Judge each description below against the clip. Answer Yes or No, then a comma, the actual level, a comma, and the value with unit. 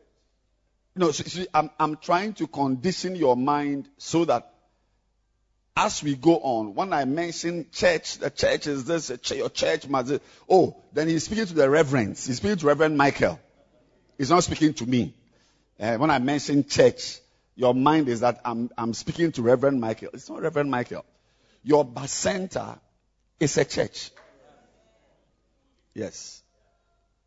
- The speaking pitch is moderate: Yes, medium, 145 Hz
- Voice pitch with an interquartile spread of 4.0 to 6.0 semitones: Yes, average, 4.4 semitones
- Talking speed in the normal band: Yes, average, 160 wpm